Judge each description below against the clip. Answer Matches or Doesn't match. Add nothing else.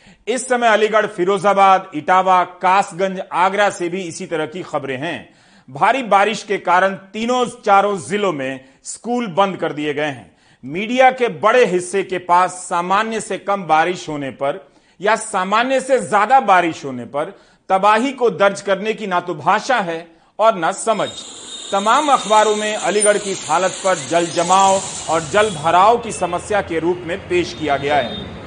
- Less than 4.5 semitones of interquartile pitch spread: Matches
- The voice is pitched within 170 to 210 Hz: Matches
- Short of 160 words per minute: Doesn't match